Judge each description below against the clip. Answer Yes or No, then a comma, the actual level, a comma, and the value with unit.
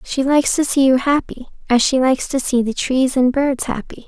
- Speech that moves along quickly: Yes, fast, 235 wpm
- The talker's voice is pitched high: Yes, very high, 265 Hz